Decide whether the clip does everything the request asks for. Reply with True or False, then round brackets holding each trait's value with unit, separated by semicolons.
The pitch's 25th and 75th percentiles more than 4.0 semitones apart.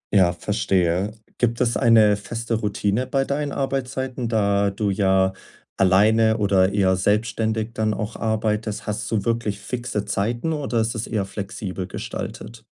False (2.6 semitones)